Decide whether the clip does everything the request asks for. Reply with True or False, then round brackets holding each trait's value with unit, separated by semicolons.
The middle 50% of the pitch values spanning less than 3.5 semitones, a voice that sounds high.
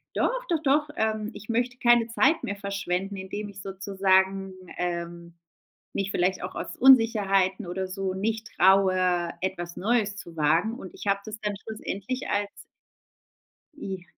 True (2.9 semitones; 195 Hz)